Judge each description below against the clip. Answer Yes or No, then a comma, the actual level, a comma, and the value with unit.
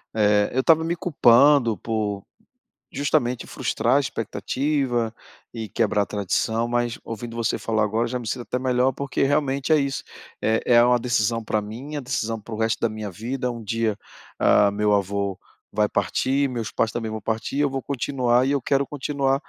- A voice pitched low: Yes, low, 120 Hz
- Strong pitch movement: No, average, 3.6 semitones